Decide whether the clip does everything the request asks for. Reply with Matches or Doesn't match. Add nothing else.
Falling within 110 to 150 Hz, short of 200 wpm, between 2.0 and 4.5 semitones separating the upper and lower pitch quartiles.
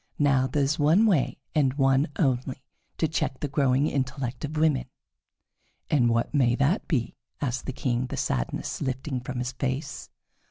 Matches